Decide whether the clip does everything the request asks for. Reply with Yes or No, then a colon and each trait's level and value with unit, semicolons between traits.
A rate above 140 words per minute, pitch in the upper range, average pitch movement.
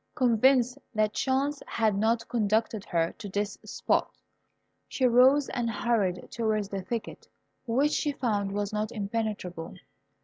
No: slow, 135 wpm; high, 220 Hz; average, 3.2 semitones